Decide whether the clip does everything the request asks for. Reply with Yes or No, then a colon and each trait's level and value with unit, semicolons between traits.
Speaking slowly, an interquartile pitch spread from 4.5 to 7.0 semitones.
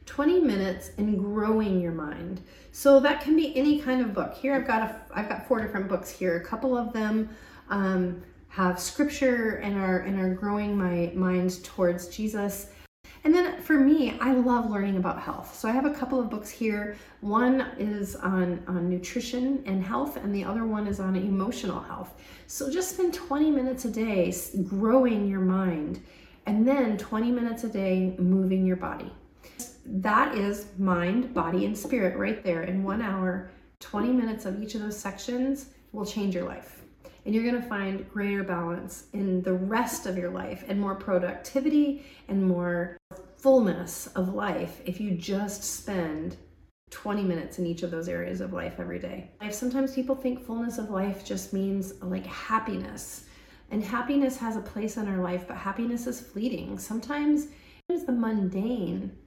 No: average, 180 wpm; average, 4.9 semitones